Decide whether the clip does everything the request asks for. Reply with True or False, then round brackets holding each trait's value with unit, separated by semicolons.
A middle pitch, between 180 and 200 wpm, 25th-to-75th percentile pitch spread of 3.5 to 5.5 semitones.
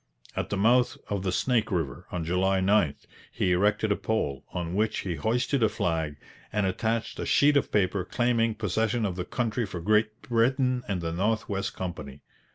False (105 Hz; 185 wpm; 4.1 semitones)